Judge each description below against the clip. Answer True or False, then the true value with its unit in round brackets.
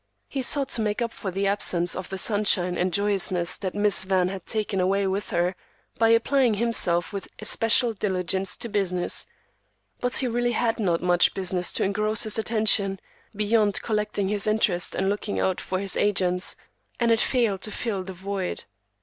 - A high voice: True (200 Hz)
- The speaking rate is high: False (180 wpm)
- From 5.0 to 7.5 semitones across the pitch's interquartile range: False (2.8 semitones)